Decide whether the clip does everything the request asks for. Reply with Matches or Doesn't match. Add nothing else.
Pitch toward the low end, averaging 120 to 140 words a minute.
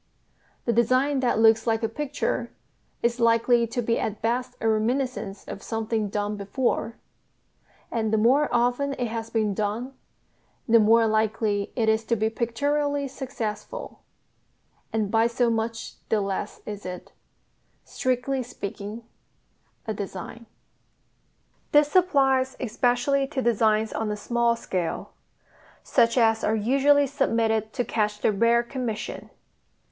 Doesn't match